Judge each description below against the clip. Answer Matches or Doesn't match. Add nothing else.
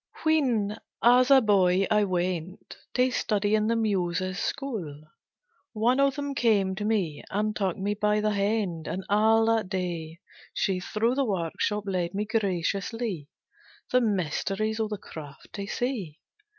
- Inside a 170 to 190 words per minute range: Doesn't match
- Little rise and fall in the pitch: Doesn't match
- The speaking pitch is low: Doesn't match